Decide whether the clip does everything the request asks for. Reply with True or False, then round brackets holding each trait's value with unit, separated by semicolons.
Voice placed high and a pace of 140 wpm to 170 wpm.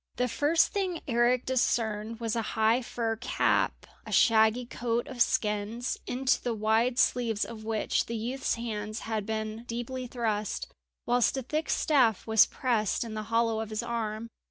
True (230 Hz; 165 wpm)